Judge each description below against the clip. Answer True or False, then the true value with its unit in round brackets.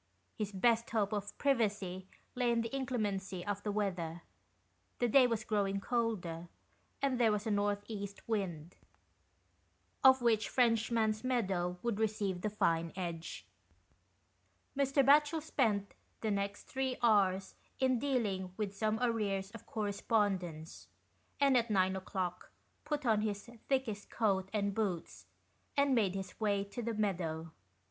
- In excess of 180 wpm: False (140 wpm)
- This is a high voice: True (210 Hz)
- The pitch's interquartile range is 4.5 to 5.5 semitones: False (3.4 semitones)